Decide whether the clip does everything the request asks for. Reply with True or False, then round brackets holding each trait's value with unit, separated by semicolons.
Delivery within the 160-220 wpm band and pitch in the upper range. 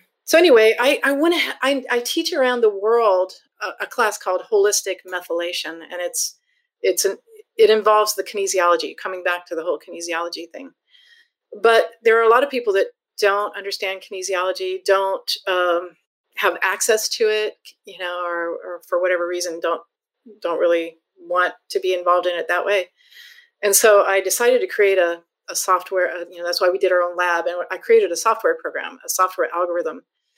True (180 wpm; 195 Hz)